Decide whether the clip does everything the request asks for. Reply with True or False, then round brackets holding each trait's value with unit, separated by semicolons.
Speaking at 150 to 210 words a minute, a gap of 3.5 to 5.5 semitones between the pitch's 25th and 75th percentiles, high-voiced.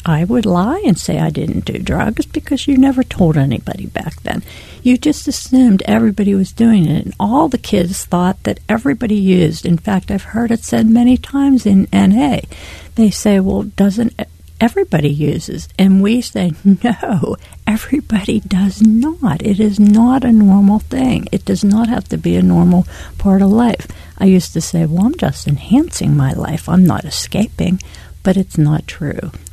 True (180 wpm; 4.5 semitones; 205 Hz)